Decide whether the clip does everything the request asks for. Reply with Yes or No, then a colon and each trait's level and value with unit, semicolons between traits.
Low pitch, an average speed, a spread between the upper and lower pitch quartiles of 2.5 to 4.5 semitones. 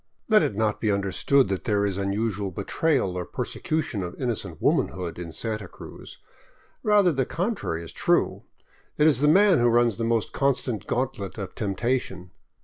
No: low, 110 Hz; average, 170 wpm; wide, 5.6 semitones